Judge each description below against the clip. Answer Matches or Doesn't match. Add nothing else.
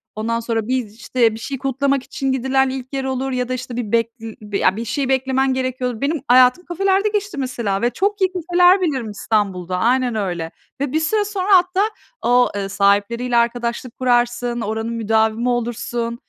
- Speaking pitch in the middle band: Doesn't match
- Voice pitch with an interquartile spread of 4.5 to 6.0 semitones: Doesn't match